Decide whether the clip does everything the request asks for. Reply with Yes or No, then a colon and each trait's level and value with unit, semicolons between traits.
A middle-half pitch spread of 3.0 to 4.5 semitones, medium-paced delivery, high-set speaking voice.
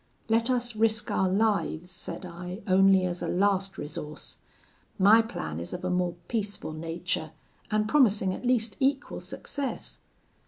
Yes: average, 3.9 semitones; average, 150 wpm; high, 195 Hz